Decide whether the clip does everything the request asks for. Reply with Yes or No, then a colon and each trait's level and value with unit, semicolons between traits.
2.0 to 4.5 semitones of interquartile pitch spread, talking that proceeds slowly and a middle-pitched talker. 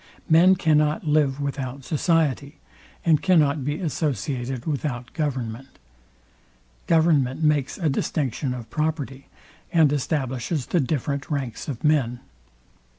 Yes: average, 3.0 semitones; slow, 110 wpm; medium, 145 Hz